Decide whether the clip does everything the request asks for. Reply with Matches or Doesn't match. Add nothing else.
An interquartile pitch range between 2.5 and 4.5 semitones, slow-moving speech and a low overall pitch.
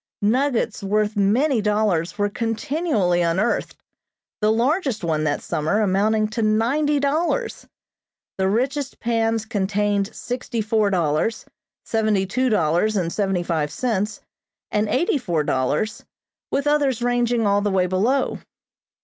Doesn't match